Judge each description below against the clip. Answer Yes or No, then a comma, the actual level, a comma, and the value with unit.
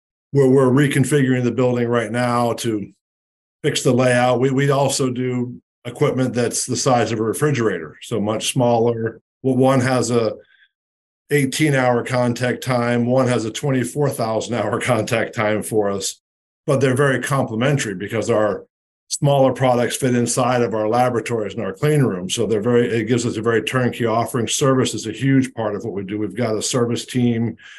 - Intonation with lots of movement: No, average, 2.7 semitones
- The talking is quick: No, average, 180 wpm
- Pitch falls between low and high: No, low, 120 Hz